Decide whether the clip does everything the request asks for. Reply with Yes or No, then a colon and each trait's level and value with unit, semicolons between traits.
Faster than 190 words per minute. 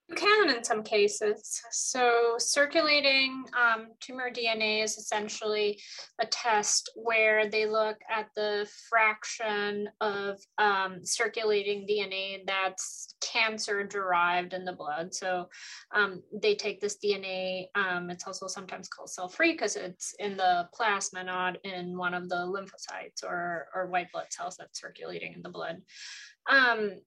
No: average, 145 wpm